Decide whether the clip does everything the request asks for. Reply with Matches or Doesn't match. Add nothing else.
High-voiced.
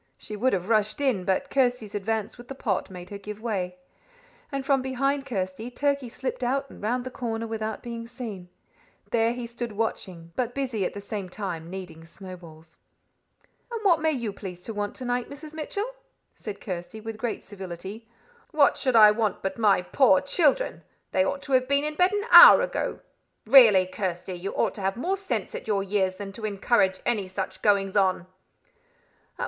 Matches